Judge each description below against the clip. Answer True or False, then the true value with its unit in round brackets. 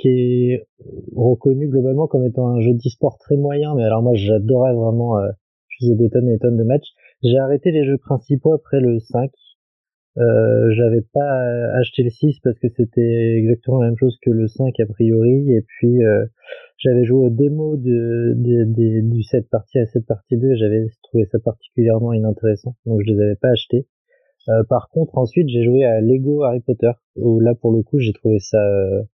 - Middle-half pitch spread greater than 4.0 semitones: False (2.5 semitones)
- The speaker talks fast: False (195 wpm)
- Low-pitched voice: True (120 Hz)